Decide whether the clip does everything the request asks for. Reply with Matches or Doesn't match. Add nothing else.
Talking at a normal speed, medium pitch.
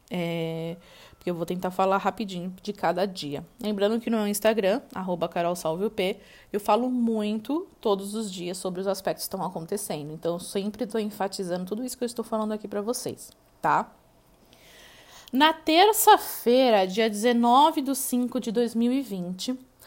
Doesn't match